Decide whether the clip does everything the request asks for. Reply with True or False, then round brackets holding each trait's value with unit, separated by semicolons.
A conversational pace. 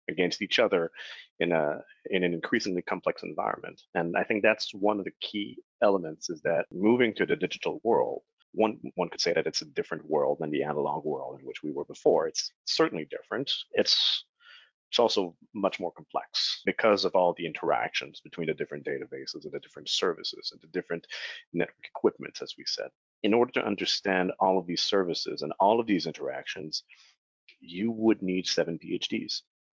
True (185 wpm)